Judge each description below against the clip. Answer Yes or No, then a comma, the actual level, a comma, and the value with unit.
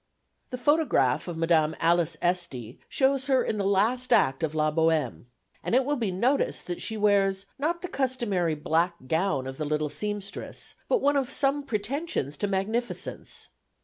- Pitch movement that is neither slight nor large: No, wide, 7.9 semitones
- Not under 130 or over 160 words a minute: No, average, 170 wpm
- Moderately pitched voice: No, high, 195 Hz